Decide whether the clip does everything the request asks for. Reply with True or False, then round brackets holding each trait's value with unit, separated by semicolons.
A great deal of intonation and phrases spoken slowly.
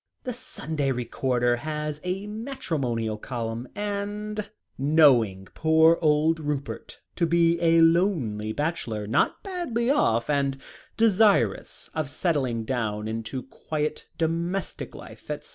True (6.5 semitones; 115 wpm)